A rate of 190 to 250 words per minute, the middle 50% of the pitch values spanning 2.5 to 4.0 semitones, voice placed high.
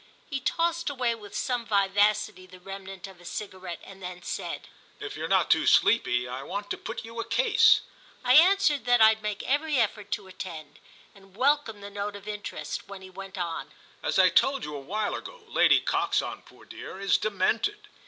No: average, 195 wpm; average, 4.5 semitones; high, 205 Hz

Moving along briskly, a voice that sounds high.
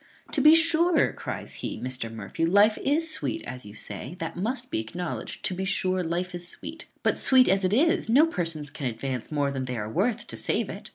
No: fast, 220 wpm; medium, 180 Hz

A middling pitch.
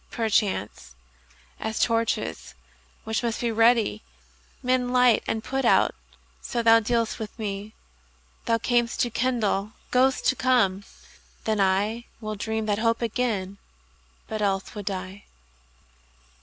No: high, 220 Hz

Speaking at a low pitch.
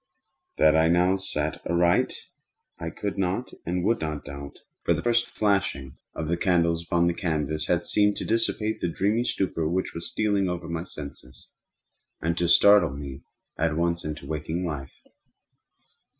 Yes: very low, 85 Hz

